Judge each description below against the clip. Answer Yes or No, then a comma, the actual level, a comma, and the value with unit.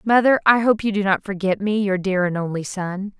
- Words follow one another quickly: Yes, fast, 245 wpm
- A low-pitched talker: No, high, 200 Hz